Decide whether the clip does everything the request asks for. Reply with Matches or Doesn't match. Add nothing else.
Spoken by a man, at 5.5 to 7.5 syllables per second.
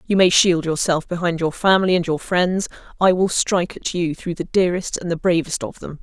Doesn't match